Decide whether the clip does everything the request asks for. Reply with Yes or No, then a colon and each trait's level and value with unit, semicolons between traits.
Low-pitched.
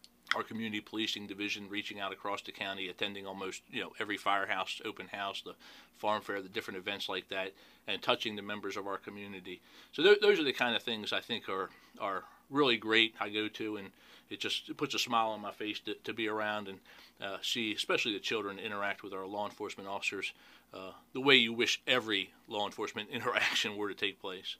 Yes: low, 105 Hz